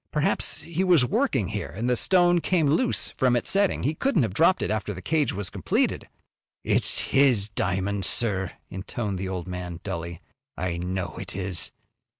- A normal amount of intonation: No, wide, 8.4 semitones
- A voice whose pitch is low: Yes, low, 105 Hz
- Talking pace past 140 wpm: Yes, average, 175 wpm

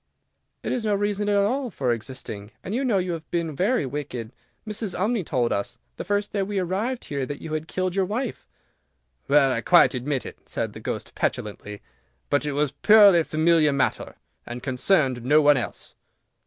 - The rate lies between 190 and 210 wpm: Yes, average, 195 wpm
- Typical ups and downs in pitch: No, wide, 7.0 semitones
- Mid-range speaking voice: Yes, medium, 160 Hz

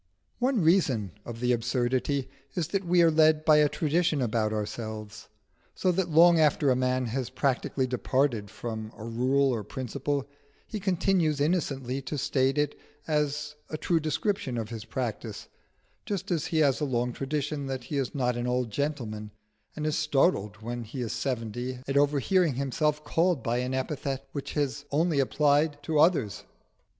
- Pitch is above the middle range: No, medium, 140 Hz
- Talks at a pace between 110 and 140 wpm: No, average, 170 wpm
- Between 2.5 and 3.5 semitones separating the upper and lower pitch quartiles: No, average, 4.0 semitones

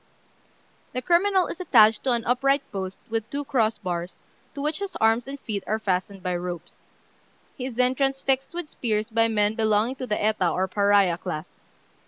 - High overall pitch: Yes, high, 225 Hz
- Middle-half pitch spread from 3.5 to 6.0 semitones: Yes, average, 5.0 semitones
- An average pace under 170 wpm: No, average, 185 wpm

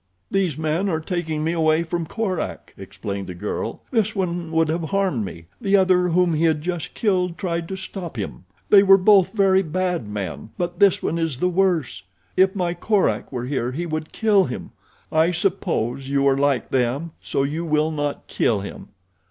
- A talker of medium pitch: Yes, medium, 165 Hz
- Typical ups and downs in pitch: Yes, average, 4.6 semitones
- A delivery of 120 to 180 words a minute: No, average, 190 wpm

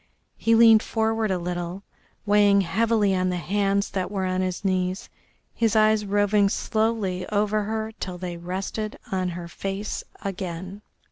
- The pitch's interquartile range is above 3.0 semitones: No, average, 2.7 semitones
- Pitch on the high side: Yes, high, 200 Hz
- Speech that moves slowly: No, average, 150 wpm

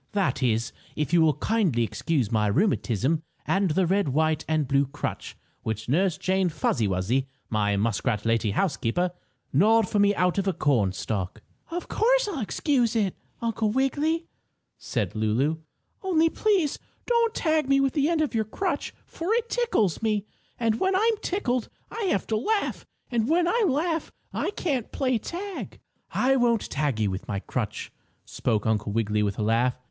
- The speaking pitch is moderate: No, high, 195 Hz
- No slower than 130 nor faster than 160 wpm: No, average, 170 wpm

